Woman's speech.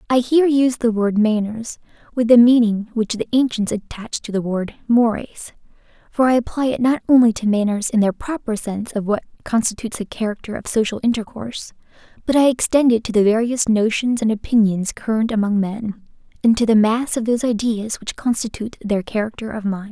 Yes: female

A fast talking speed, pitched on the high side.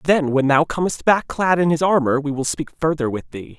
No: fast, 250 wpm; medium, 155 Hz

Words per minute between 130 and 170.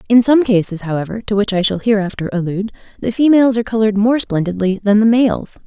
No: average, 200 wpm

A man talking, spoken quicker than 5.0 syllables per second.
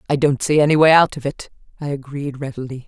No: female; 6.3 syllables/s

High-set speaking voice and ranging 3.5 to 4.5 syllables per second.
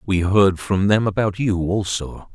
No: low, 100 Hz; 4.1 syllables/s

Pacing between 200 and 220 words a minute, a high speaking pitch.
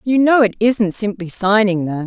Yes: fast, 205 wpm; high, 210 Hz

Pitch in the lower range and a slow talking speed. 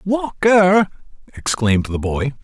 No: medium, 150 Hz; slow, 125 wpm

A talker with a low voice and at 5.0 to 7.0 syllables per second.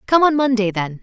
No: high, 235 Hz; 5.6 syllables/s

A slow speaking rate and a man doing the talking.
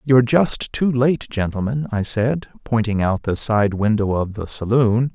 No: average, 175 wpm; male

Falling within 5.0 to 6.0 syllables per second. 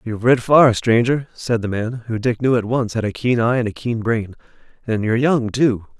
Yes: 5.1 syllables/s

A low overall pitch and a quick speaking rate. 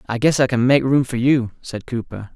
Yes: low, 125 Hz; fast, 255 wpm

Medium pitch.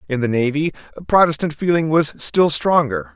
Yes: medium, 145 Hz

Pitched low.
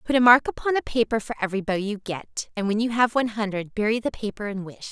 No: high, 215 Hz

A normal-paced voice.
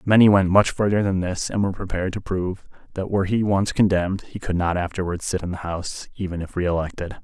No: fast, 225 wpm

